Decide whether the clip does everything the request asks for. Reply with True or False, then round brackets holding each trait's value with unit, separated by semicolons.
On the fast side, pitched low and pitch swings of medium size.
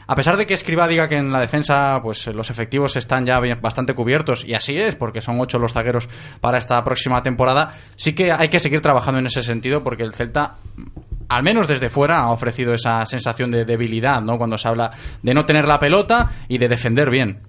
True (220 wpm; 125 Hz; 3.4 semitones)